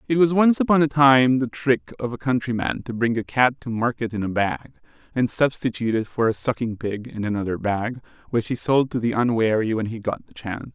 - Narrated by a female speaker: No, male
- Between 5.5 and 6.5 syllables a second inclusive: Yes, 5.6 syllables/s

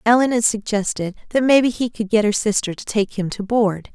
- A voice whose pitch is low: No, high, 215 Hz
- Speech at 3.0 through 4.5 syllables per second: No, 5.4 syllables/s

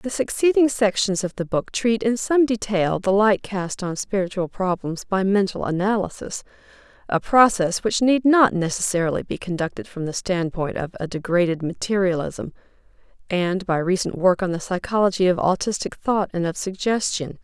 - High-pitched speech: Yes, high, 195 Hz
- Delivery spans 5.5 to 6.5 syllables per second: No, 5.0 syllables/s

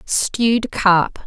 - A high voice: Yes, high, 205 Hz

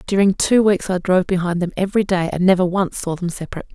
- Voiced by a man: No, female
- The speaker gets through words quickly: Yes, fast, 240 wpm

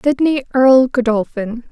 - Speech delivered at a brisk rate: No, slow, 105 wpm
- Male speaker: No, female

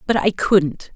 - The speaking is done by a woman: Yes, female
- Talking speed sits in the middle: Yes, average, 190 wpm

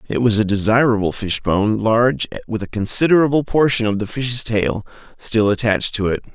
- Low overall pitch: Yes, low, 115 Hz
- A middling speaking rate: Yes, average, 170 wpm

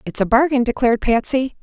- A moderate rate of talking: Yes, average, 185 wpm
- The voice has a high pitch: Yes, high, 245 Hz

